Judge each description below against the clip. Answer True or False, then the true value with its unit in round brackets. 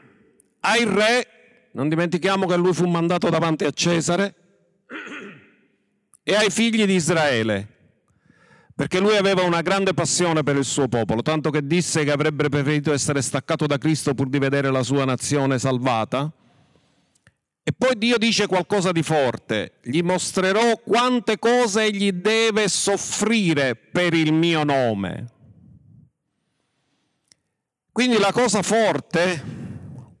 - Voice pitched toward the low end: False (170 Hz)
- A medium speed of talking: True (130 wpm)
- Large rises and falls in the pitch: True (6.2 semitones)